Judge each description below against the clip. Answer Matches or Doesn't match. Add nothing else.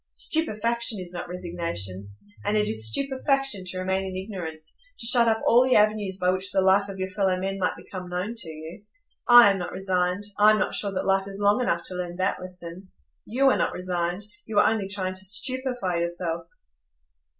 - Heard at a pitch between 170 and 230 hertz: Matches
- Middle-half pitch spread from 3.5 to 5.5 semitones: Doesn't match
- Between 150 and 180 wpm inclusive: Doesn't match